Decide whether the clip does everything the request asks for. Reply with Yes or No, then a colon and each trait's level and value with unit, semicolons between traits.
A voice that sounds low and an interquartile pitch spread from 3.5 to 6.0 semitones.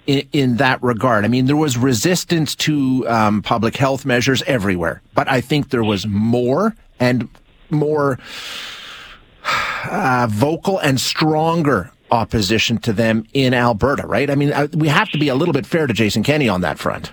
Yes: low, 130 Hz; average, 4.0 semitones